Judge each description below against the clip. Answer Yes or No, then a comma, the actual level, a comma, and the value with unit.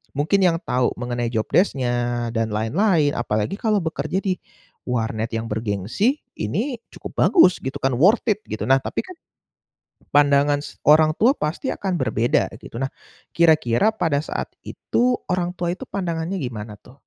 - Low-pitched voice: No, medium, 145 Hz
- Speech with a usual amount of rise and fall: No, wide, 7.5 semitones